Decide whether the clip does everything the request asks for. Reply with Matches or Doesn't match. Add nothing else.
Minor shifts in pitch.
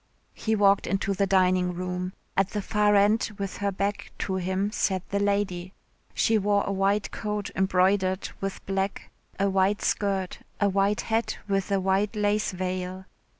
Matches